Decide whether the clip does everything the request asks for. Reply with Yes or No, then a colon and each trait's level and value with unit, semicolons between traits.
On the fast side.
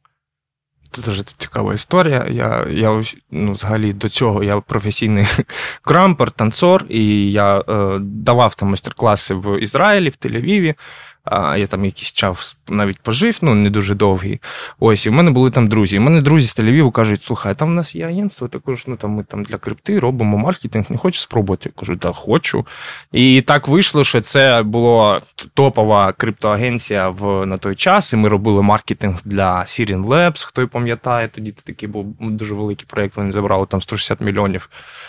Yes: fast, 180 wpm